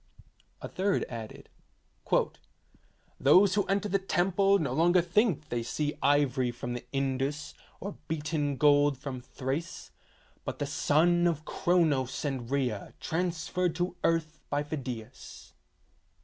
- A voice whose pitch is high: No, medium, 150 Hz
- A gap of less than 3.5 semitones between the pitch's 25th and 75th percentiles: No, average, 4.6 semitones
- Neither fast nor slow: No, slow, 130 wpm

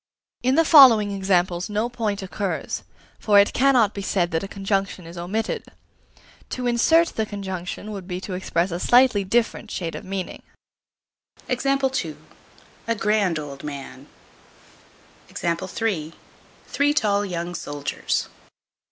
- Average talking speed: No, slow, 125 wpm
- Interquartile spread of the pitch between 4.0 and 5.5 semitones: Yes, average, 4.4 semitones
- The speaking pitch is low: No, high, 200 Hz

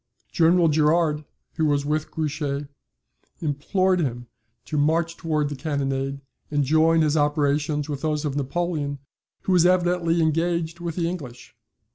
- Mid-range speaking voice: Yes, medium, 155 Hz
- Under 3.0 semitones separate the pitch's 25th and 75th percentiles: Yes, narrow, 2.6 semitones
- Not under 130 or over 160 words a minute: Yes, average, 140 wpm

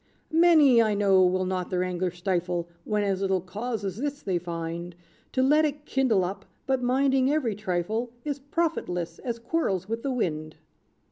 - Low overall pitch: No, high, 205 Hz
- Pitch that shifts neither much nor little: No, wide, 6.5 semitones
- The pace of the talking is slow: No, average, 175 wpm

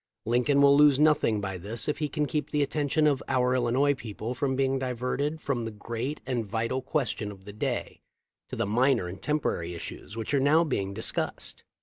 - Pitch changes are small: No, average, 4.3 semitones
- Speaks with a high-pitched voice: No, low, 130 Hz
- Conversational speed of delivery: No, fast, 215 wpm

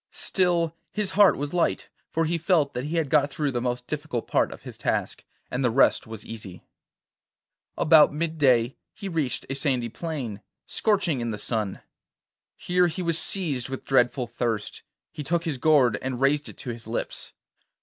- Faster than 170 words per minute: Yes, average, 180 wpm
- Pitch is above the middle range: No, medium, 145 Hz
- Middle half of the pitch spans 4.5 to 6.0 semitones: Yes, average, 5.2 semitones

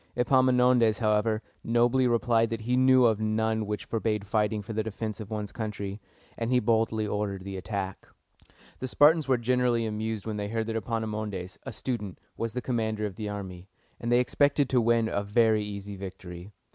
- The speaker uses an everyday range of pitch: No, narrow, 2.3 semitones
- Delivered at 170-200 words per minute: Yes, average, 185 wpm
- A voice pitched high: No, low, 110 Hz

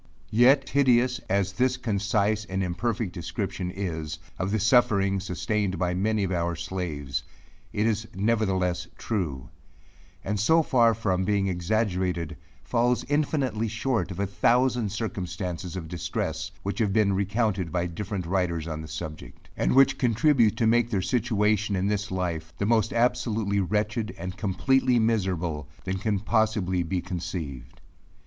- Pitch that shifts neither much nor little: Yes, average, 3.8 semitones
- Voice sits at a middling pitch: No, low, 100 Hz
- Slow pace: No, average, 145 wpm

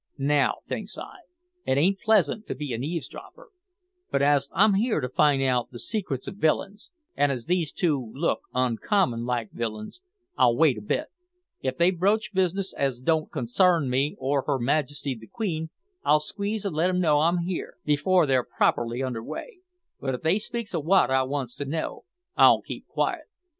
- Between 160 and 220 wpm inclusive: Yes, average, 185 wpm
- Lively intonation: Yes, wide, 6.0 semitones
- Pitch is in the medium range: Yes, medium, 150 Hz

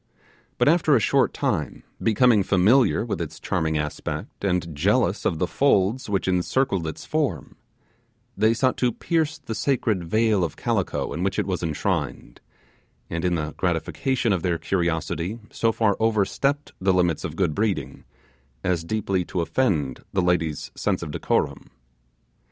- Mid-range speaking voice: No, very low, 95 Hz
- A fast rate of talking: No, average, 155 wpm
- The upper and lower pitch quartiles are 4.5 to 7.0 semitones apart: Yes, average, 5.1 semitones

